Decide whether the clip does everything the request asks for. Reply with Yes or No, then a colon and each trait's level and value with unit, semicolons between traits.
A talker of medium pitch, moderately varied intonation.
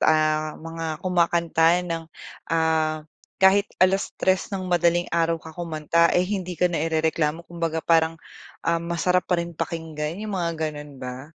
No: medium, 165 Hz; narrow, 1.8 semitones